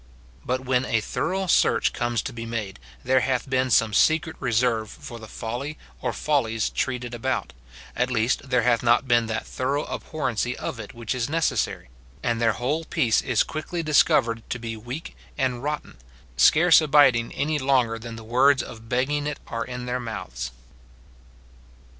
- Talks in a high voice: No, low, 125 Hz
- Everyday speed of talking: Yes, average, 170 wpm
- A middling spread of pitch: Yes, average, 3.3 semitones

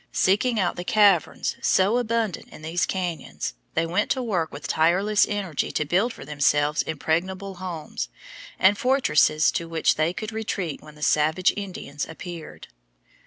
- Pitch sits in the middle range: Yes, medium, 180 Hz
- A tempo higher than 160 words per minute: No, average, 155 wpm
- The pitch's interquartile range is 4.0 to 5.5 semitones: Yes, average, 4.5 semitones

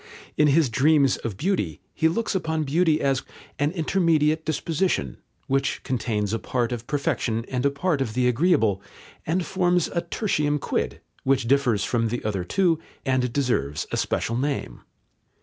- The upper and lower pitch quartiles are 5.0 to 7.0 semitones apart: Yes, average, 5.3 semitones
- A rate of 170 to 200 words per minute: No, average, 160 wpm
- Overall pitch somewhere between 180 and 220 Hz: No, medium, 140 Hz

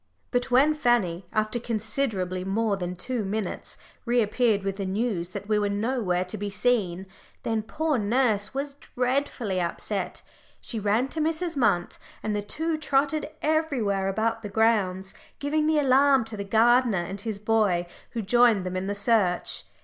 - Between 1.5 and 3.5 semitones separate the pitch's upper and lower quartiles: No, average, 4.4 semitones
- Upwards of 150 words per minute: Yes, average, 165 wpm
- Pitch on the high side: Yes, high, 220 Hz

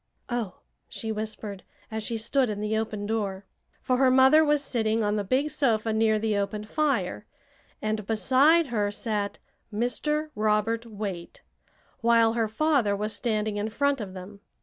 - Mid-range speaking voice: No, high, 220 Hz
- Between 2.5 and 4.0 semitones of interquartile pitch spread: Yes, average, 3.1 semitones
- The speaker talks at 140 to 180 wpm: Yes, average, 160 wpm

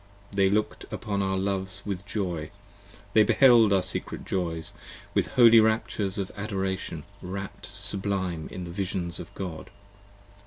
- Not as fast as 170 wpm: Yes, average, 140 wpm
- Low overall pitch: Yes, very low, 95 Hz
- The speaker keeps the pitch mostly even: Yes, narrow, 1.8 semitones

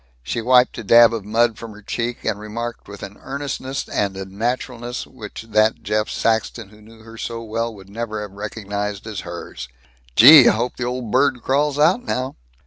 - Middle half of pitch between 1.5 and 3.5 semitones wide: Yes, average, 2.8 semitones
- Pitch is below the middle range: Yes, low, 115 Hz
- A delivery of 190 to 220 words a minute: Yes, average, 195 wpm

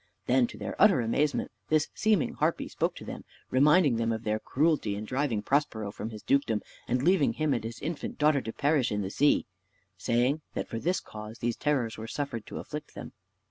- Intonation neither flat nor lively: Yes, average, 4.8 semitones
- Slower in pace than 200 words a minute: No, fast, 205 wpm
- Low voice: Yes, low, 125 Hz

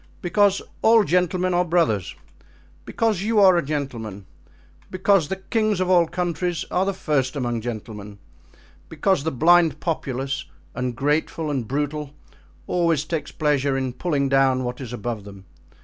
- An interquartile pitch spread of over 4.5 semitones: Yes, wide, 5.6 semitones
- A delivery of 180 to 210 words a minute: No, average, 145 wpm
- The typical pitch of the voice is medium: Yes, medium, 150 Hz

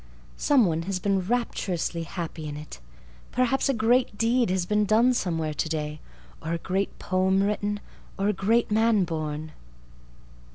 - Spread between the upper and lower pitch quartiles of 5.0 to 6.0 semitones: Yes, average, 5.3 semitones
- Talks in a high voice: Yes, high, 195 Hz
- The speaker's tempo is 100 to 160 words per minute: Yes, average, 140 wpm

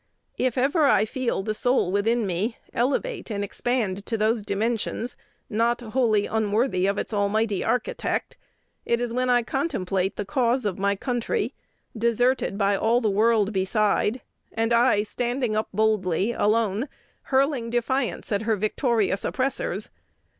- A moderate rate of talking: Yes, average, 145 wpm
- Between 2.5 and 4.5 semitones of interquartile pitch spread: Yes, average, 3.1 semitones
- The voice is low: No, high, 225 Hz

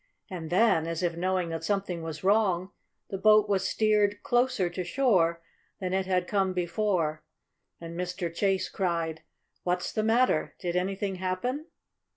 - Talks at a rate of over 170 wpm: No, average, 155 wpm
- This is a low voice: No, medium, 185 Hz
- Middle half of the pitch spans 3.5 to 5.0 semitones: No, average, 3.1 semitones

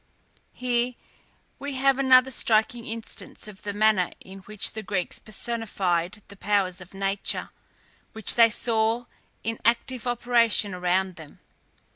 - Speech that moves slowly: Yes, slow, 130 wpm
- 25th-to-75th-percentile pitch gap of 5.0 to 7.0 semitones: No, average, 3.6 semitones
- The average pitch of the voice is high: Yes, high, 220 Hz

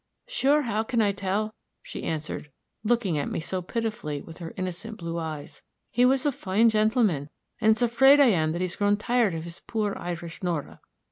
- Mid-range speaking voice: No, high, 205 Hz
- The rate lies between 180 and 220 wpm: Yes, average, 195 wpm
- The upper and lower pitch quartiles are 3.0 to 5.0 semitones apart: No, wide, 5.4 semitones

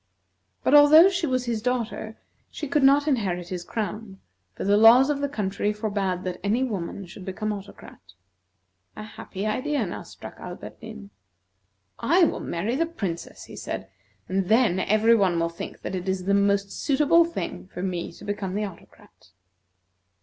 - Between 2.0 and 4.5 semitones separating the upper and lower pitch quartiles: No, average, 5.2 semitones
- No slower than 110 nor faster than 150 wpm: No, average, 165 wpm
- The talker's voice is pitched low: No, high, 210 Hz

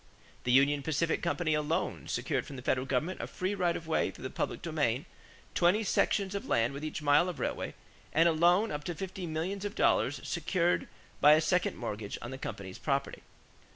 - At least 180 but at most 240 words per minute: Yes, average, 200 wpm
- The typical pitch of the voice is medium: Yes, medium, 160 Hz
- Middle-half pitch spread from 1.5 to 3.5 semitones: No, average, 4.5 semitones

